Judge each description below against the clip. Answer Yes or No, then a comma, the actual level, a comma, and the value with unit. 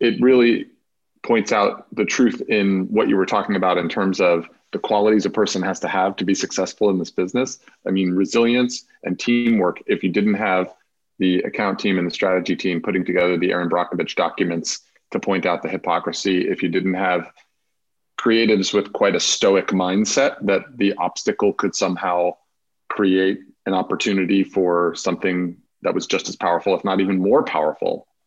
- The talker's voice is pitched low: Yes, very low, 95 Hz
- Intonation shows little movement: Yes, narrow, 2.3 semitones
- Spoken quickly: No, average, 180 wpm